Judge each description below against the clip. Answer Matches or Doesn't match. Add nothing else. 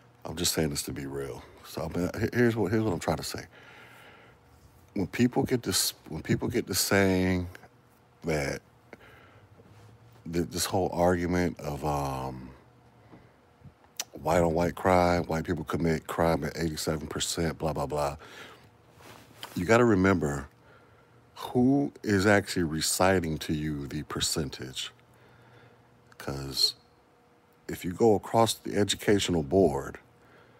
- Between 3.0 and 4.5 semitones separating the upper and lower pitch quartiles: Doesn't match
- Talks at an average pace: Doesn't match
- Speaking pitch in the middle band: Doesn't match